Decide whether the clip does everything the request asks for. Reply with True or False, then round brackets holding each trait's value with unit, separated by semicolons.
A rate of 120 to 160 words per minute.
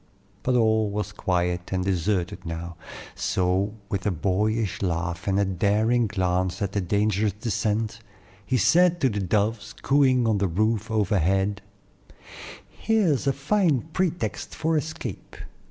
True (140 wpm)